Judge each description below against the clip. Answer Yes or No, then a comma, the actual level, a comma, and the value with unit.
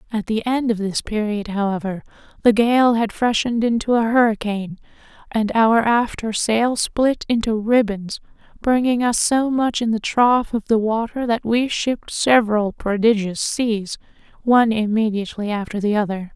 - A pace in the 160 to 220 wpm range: No, average, 150 wpm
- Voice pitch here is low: No, high, 225 Hz